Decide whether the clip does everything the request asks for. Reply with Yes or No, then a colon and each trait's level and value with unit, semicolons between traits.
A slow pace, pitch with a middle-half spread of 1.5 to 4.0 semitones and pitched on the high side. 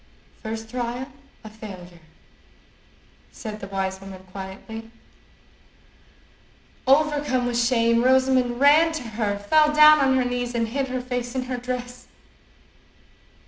Yes: slow, 125 wpm; average, 3.0 semitones; high, 245 Hz